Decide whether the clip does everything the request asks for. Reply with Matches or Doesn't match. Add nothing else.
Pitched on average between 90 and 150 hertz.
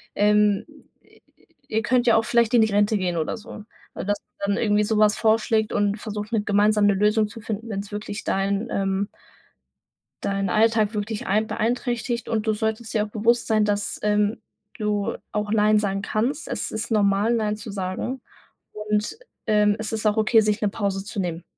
Doesn't match